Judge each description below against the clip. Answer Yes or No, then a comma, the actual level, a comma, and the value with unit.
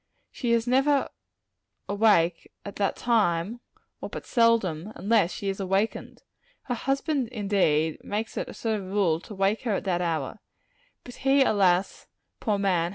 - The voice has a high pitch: Yes, high, 205 Hz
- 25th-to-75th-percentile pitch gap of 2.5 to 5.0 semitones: Yes, average, 4.0 semitones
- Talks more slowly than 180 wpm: Yes, average, 160 wpm